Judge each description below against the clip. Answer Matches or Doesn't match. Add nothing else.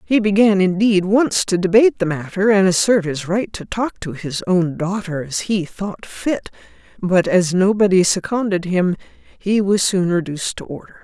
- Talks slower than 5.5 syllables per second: Matches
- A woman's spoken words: Matches